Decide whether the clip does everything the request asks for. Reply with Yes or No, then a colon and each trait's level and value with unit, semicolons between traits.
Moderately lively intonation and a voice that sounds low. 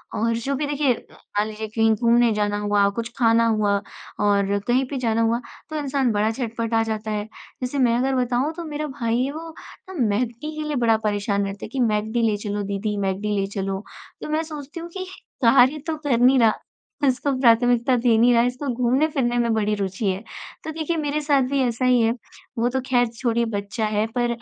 No: average, 3.8 semitones; high, 235 Hz